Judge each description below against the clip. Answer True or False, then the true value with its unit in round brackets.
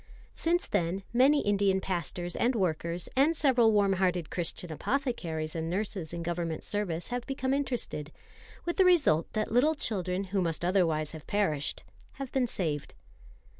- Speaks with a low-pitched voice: False (190 Hz)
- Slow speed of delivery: False (155 wpm)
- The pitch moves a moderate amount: False (6.7 semitones)